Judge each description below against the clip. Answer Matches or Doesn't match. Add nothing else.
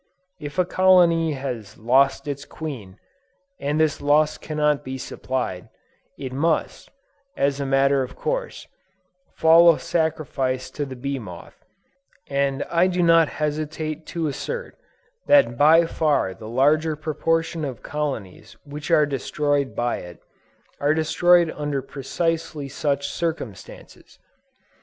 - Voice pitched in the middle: Matches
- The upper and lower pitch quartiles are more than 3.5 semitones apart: Doesn't match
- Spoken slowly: Matches